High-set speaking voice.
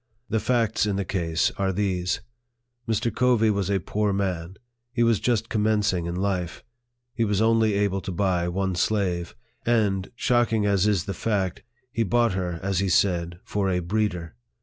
No: low, 100 Hz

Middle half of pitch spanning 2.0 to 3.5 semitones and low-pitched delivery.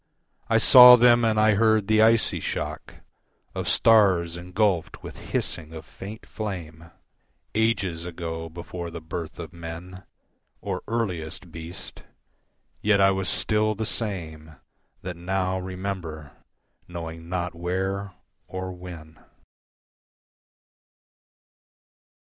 No: average, 3.9 semitones; very low, 90 Hz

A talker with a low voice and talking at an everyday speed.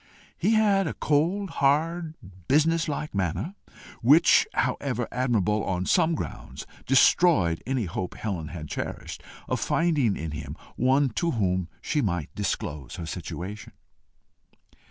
No: low, 125 Hz; slow, 130 wpm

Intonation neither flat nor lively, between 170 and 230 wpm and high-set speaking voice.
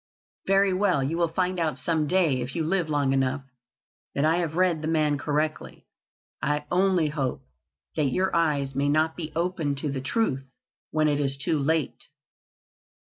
No: average, 3.4 semitones; average, 175 wpm; medium, 155 Hz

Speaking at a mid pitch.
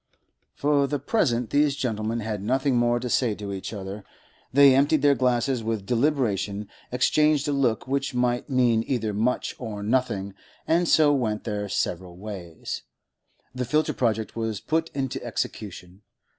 No: low, 120 Hz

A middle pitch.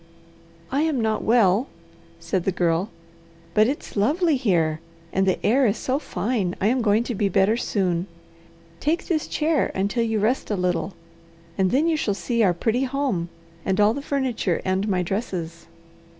No: high, 215 Hz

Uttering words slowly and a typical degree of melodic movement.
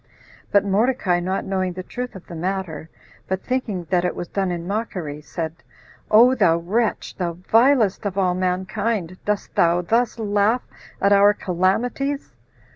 No: average, 155 wpm; average, 3.7 semitones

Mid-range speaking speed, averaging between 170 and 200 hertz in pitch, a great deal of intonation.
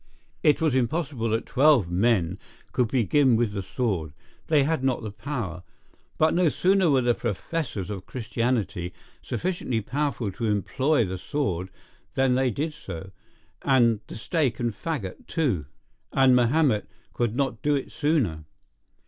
No: average, 150 wpm; low, 125 Hz; wide, 5.9 semitones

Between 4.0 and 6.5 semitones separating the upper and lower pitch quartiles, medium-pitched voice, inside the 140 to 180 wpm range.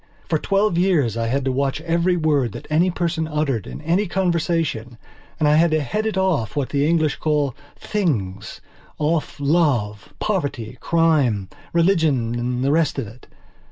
Yes: average, 4.9 semitones; medium, 150 Hz; average, 160 wpm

